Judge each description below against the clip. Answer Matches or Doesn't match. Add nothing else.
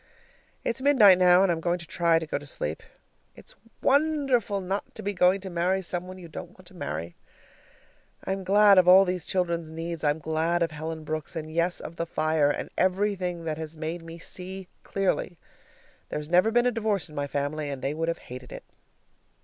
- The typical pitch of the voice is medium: Matches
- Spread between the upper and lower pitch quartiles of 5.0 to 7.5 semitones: Doesn't match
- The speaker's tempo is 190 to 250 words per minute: Matches